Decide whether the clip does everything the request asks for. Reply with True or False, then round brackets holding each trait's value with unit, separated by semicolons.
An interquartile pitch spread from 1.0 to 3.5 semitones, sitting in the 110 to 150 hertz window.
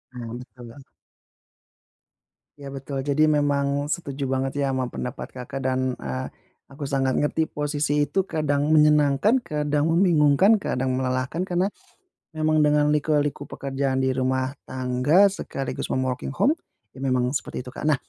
True (2.4 semitones; 140 Hz)